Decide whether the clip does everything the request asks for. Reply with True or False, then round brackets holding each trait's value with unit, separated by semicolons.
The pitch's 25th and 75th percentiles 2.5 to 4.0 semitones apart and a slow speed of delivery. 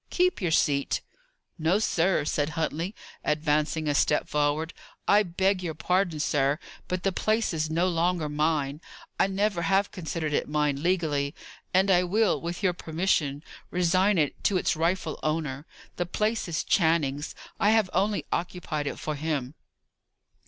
False (3.7 semitones; 155 wpm)